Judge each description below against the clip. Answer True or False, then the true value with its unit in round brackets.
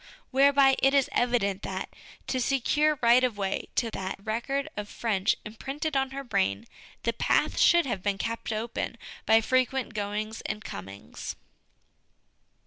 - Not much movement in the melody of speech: False (4.5 semitones)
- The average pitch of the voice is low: False (235 Hz)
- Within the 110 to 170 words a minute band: True (145 wpm)